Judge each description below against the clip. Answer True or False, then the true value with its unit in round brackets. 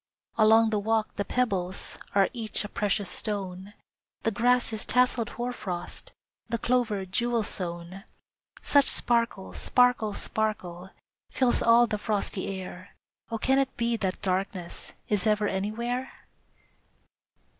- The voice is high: True (215 Hz)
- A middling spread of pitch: True (3.5 semitones)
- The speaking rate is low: True (125 wpm)